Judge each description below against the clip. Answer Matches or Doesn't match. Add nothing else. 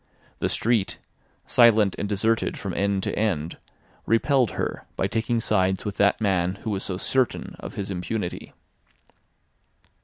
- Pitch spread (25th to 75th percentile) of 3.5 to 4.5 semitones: Doesn't match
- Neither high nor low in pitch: Doesn't match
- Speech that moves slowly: Doesn't match